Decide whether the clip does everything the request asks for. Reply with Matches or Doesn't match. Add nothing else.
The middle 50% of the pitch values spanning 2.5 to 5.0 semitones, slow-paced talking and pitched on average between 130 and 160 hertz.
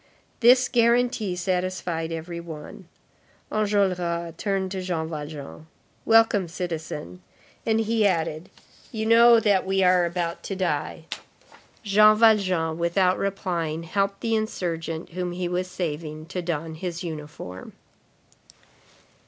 Doesn't match